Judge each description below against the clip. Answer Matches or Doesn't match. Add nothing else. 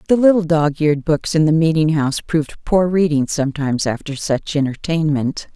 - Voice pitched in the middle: Matches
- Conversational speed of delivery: Matches